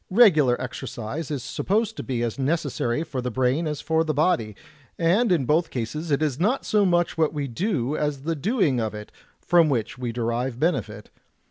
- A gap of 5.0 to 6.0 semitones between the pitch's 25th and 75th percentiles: Yes, average, 5.3 semitones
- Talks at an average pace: Yes, average, 195 wpm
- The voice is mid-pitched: Yes, medium, 150 Hz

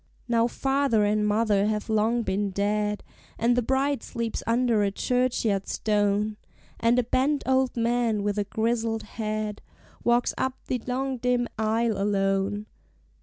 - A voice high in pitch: Yes, high, 225 Hz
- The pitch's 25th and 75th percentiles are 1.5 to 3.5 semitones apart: Yes, average, 2.8 semitones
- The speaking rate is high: No, average, 145 wpm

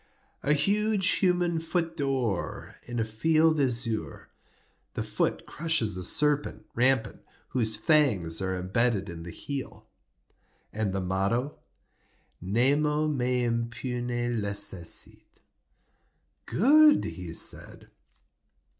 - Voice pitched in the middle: No, low, 125 Hz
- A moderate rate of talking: No, slow, 100 wpm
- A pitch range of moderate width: No, wide, 6.5 semitones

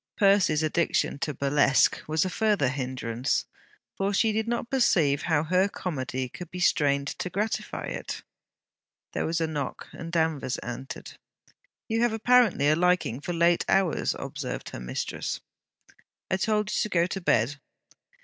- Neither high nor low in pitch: Yes, medium, 170 Hz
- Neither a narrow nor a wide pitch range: No, wide, 5.7 semitones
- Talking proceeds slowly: No, average, 155 wpm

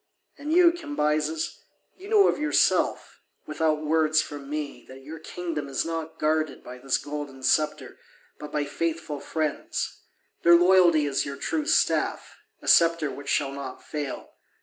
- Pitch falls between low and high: Yes, medium, 155 Hz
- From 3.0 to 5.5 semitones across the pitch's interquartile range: No, narrow, 2.6 semitones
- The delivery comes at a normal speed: Yes, average, 150 wpm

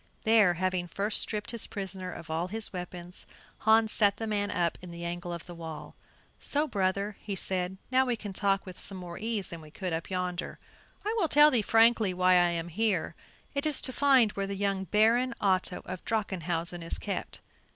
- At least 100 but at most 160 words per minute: No, average, 200 wpm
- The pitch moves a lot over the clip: No, average, 3.8 semitones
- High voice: Yes, high, 195 Hz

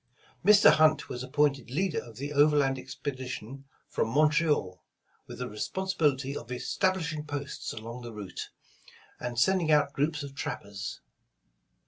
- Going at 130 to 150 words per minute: Yes, average, 140 wpm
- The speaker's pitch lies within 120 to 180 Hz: Yes, medium, 140 Hz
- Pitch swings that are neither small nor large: Yes, average, 3.7 semitones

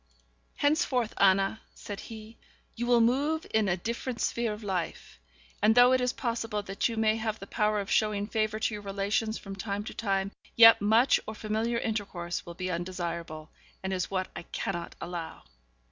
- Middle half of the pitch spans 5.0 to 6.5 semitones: No, average, 2.8 semitones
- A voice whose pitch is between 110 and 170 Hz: No, high, 215 Hz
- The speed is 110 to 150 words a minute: No, average, 180 wpm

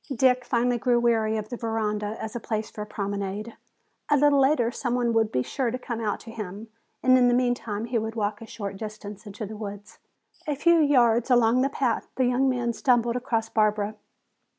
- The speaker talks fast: Yes, fast, 210 wpm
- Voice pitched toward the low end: No, high, 230 Hz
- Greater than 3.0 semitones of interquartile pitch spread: No, average, 2.7 semitones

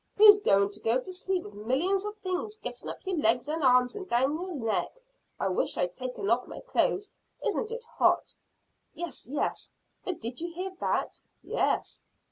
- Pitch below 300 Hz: No, very high, 315 Hz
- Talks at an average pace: Yes, average, 180 wpm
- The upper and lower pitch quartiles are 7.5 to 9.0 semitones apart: Yes, wide, 8.0 semitones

